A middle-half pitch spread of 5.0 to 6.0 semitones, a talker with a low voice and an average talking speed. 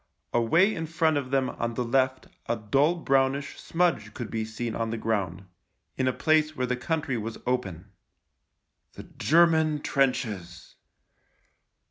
Yes: wide, 5.4 semitones; low, 130 Hz; average, 150 wpm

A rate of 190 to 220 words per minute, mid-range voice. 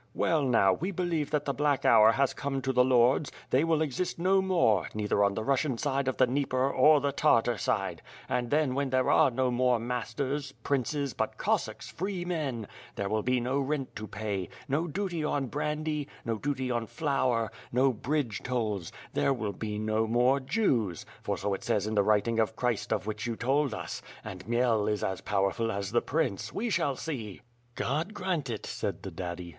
No: average, 200 wpm; low, 130 Hz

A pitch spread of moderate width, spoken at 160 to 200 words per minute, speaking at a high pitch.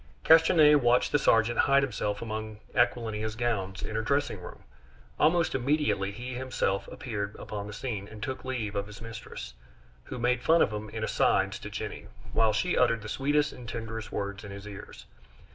No: average, 3.8 semitones; average, 180 wpm; low, 115 Hz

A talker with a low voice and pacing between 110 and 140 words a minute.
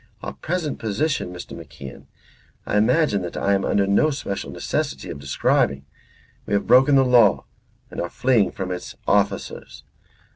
No: low, 100 Hz; average, 160 wpm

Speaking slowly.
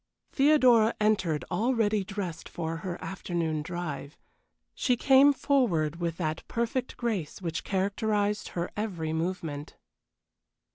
Yes: slow, 110 wpm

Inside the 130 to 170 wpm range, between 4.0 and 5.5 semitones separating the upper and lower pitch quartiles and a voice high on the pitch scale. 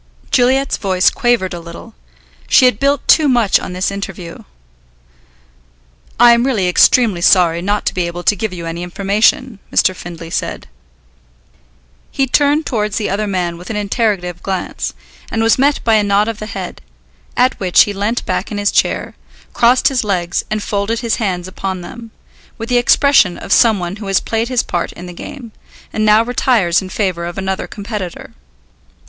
No: average, 180 wpm; average, 4.3 semitones; high, 205 Hz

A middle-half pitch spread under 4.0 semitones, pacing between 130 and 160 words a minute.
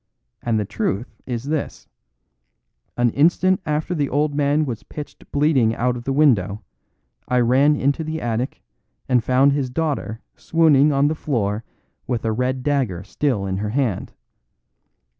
No: average, 4.3 semitones; average, 155 wpm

